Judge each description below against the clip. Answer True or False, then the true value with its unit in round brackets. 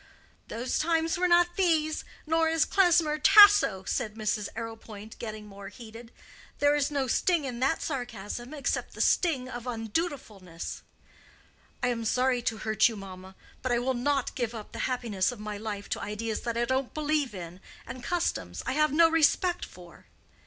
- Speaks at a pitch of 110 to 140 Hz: False (245 Hz)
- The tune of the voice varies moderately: False (6.0 semitones)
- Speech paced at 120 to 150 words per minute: False (175 wpm)